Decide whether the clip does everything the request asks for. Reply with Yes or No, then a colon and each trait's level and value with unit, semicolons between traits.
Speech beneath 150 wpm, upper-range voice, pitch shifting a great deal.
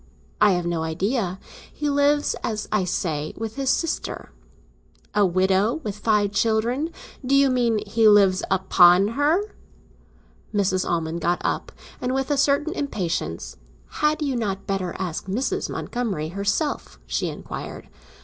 Yes: average, 140 wpm; high, 210 Hz; wide, 6.0 semitones